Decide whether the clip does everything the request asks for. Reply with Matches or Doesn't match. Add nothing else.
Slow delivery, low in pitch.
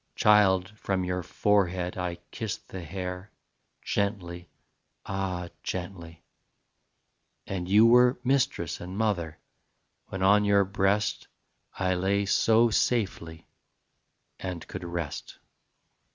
Matches